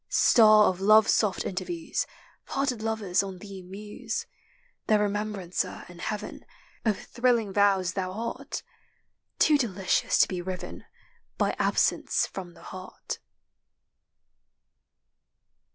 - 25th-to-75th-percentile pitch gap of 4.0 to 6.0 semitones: No, average, 2.8 semitones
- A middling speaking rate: No, slow, 110 wpm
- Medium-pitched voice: No, high, 205 Hz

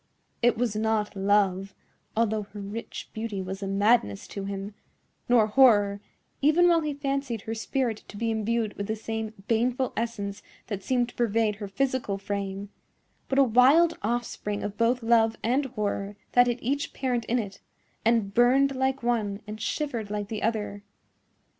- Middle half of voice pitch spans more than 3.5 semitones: No, average, 3.2 semitones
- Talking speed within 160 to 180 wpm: Yes, average, 165 wpm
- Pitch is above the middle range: Yes, high, 225 Hz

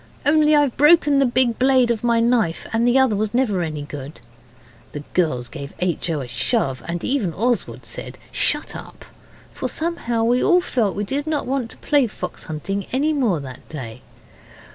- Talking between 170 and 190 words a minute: Yes, average, 185 wpm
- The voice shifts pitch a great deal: Yes, wide, 8.0 semitones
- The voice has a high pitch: Yes, high, 235 Hz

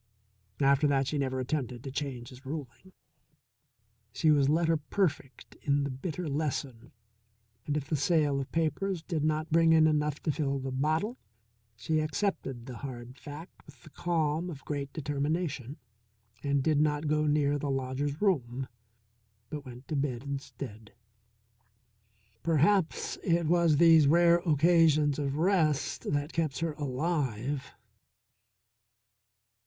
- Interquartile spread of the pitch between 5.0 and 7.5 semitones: No, average, 2.8 semitones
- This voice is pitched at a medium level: Yes, medium, 145 Hz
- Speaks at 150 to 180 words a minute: No, average, 140 wpm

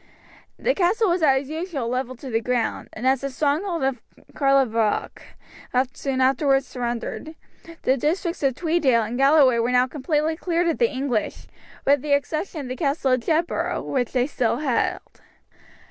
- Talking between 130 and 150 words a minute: No, average, 160 wpm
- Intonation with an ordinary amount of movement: Yes, average, 3.9 semitones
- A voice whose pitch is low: No, very high, 275 Hz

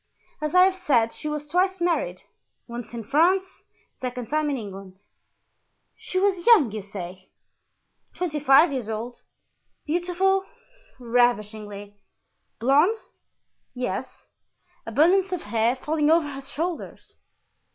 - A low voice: No, very high, 285 Hz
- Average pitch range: No, wide, 7.5 semitones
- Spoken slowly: Yes, slow, 120 wpm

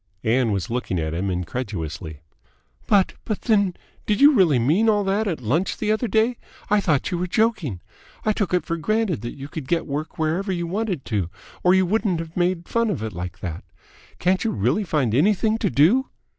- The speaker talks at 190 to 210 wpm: Yes, fast, 205 wpm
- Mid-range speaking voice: Yes, medium, 175 Hz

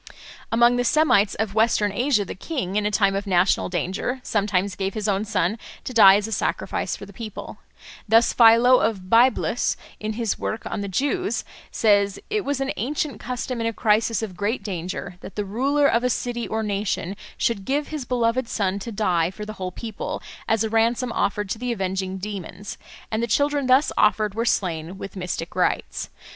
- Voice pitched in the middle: No, high, 215 Hz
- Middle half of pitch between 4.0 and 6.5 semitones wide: No, average, 3.4 semitones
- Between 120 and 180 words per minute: No, average, 195 wpm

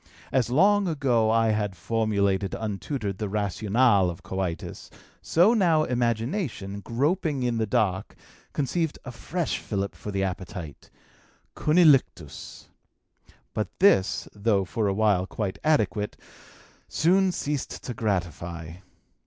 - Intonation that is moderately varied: No, wide, 6.2 semitones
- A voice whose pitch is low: Yes, low, 110 Hz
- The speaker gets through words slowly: Yes, slow, 120 wpm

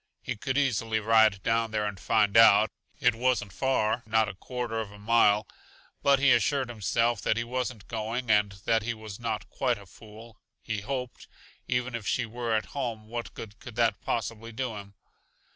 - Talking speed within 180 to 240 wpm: Yes, average, 190 wpm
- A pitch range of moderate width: No, narrow, 2.2 semitones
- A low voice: Yes, low, 115 Hz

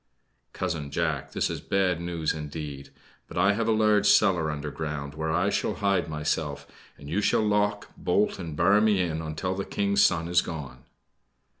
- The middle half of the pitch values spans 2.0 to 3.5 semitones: No, average, 4.7 semitones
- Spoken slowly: No, average, 175 wpm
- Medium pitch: No, very low, 85 Hz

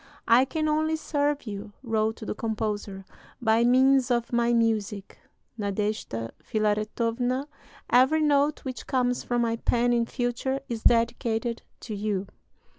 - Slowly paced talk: Yes, slow, 130 wpm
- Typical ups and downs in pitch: Yes, average, 3.1 semitones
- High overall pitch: Yes, high, 235 Hz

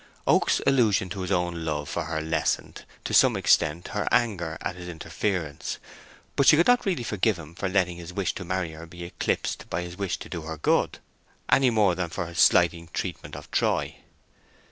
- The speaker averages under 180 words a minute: No, average, 200 wpm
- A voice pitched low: Yes, very low, 90 Hz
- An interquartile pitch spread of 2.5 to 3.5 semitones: Yes, average, 2.9 semitones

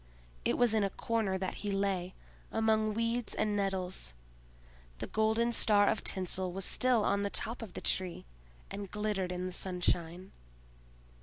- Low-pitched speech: No, high, 200 Hz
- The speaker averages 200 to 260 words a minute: No, average, 160 wpm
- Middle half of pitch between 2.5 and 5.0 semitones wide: Yes, average, 2.9 semitones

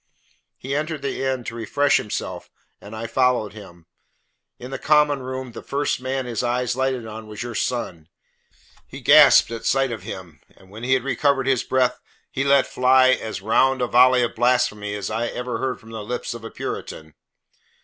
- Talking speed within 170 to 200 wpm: Yes, average, 190 wpm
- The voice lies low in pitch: Yes, low, 125 Hz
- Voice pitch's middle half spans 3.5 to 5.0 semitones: No, average, 3.0 semitones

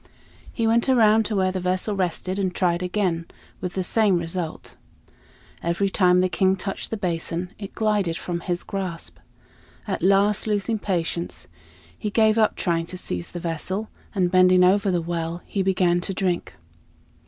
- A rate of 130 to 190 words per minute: Yes, average, 165 wpm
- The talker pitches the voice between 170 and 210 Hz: Yes, medium, 185 Hz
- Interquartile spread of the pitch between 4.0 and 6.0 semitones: No, narrow, 2.5 semitones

